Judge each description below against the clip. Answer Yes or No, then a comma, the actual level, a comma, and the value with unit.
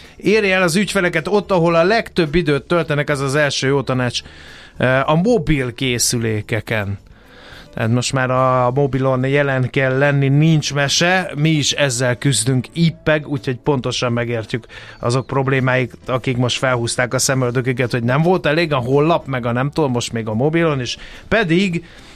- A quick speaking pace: Yes, fast, 160 wpm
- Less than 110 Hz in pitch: No, low, 135 Hz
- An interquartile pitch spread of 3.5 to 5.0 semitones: Yes, average, 4.0 semitones